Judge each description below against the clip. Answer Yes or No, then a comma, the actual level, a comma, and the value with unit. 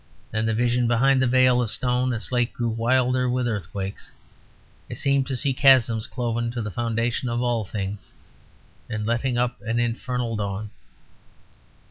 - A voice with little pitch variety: Yes, narrow, 2.0 semitones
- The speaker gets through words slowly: No, average, 160 wpm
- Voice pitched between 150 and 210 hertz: No, low, 120 Hz